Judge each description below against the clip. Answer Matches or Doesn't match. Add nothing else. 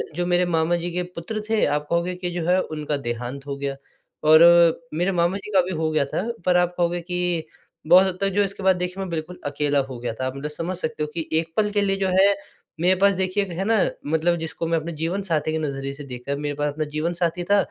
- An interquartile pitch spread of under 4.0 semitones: Matches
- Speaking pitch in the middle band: Matches